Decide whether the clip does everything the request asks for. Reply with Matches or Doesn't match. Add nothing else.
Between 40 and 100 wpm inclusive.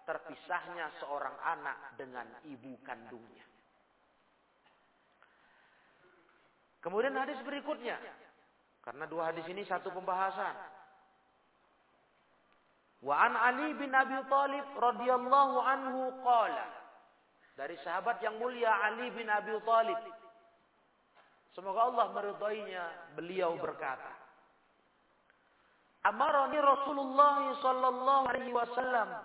Matches